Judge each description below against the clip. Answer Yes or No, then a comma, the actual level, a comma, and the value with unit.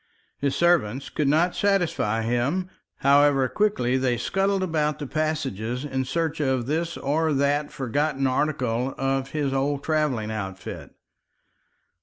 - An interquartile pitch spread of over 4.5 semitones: No, average, 3.4 semitones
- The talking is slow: Yes, slow, 130 wpm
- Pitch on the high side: No, medium, 140 Hz